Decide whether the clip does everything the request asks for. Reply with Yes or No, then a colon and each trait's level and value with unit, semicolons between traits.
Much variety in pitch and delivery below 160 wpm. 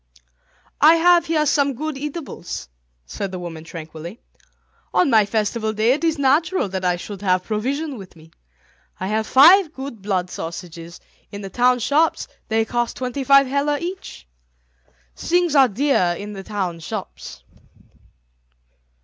Yes: wide, 7.4 semitones; average, 150 wpm